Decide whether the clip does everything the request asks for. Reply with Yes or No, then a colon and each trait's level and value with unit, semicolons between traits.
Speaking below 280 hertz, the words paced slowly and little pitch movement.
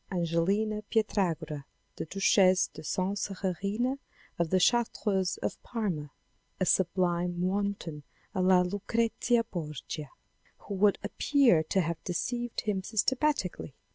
No: high, 190 Hz; slow, 120 wpm; average, 3.6 semitones